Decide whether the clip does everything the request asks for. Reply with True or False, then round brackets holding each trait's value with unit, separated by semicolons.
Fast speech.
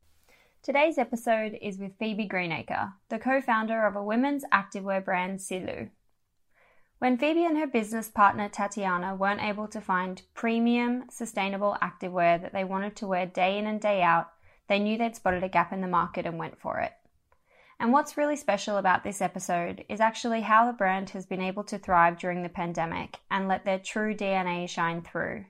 False (185 wpm)